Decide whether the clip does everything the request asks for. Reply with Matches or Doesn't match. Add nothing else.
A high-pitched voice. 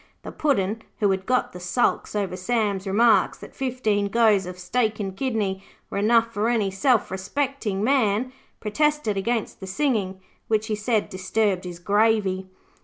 Matches